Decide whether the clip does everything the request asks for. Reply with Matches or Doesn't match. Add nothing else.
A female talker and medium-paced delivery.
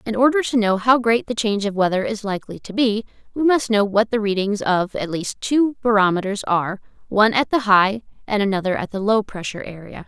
Doesn't match